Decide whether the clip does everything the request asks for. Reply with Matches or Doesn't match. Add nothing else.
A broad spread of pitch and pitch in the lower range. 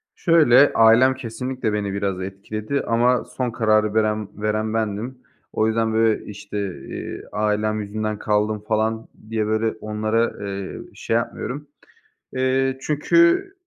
Doesn't match